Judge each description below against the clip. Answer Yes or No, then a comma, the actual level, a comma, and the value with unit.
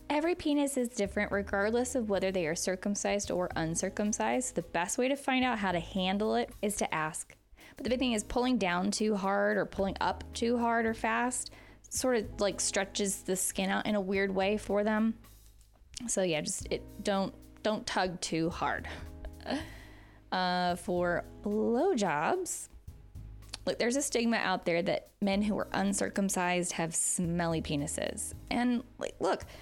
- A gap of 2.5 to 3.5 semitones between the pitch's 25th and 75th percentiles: No, average, 4.4 semitones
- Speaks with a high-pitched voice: Yes, high, 200 Hz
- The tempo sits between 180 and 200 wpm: No, average, 170 wpm